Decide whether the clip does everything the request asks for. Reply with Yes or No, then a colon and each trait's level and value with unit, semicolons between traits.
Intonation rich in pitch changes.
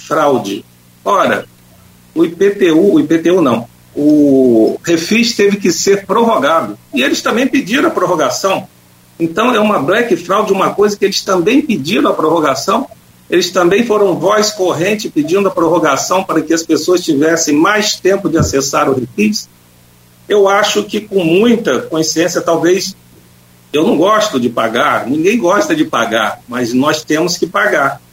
Yes: wide, 6.4 semitones